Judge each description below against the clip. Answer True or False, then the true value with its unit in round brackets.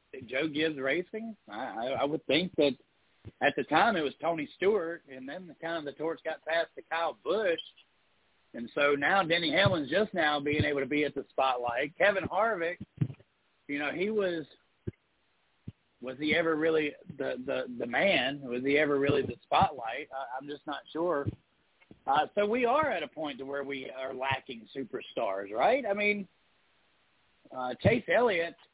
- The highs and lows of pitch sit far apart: False (4.4 semitones)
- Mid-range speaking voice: True (150 Hz)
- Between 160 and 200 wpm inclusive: True (175 wpm)